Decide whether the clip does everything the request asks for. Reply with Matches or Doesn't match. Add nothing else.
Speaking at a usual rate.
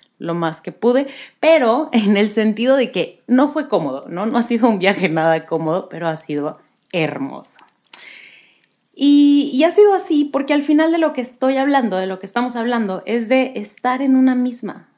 Doesn't match